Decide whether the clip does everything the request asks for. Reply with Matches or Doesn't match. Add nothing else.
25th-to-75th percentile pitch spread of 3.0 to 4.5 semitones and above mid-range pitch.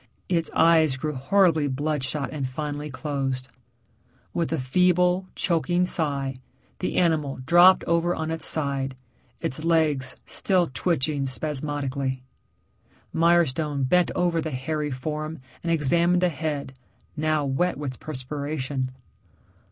Doesn't match